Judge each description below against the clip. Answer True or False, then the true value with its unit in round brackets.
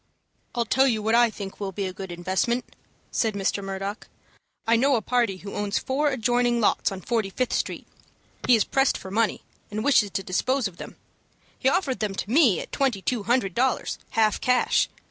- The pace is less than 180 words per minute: False (200 wpm)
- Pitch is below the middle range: False (225 Hz)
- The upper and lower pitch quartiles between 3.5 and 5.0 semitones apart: True (4.2 semitones)